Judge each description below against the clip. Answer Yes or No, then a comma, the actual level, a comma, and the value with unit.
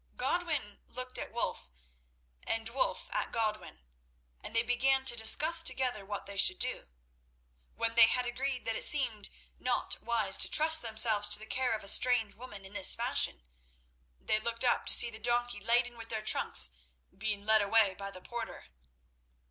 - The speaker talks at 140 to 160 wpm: No, average, 175 wpm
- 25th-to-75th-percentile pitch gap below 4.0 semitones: Yes, average, 2.8 semitones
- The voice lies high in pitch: Yes, high, 230 Hz